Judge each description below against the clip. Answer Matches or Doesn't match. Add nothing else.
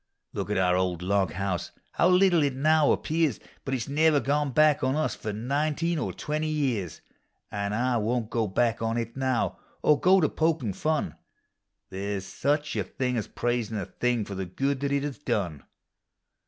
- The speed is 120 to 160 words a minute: Doesn't match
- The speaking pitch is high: Doesn't match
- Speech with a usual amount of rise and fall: Doesn't match